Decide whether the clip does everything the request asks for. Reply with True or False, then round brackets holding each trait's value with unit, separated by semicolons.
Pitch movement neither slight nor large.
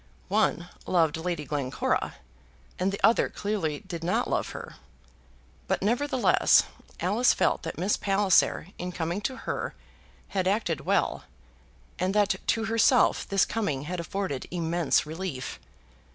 True (4.0 semitones)